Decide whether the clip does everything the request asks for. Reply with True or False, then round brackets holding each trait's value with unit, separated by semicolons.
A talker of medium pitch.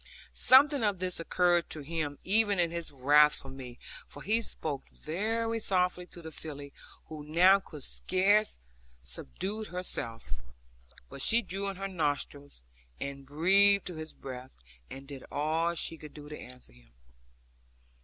True (165 Hz)